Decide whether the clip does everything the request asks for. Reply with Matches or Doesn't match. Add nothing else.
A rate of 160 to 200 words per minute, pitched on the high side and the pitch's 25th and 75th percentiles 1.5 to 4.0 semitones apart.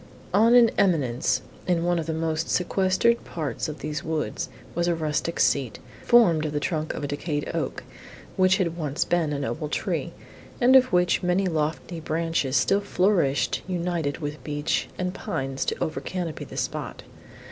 Doesn't match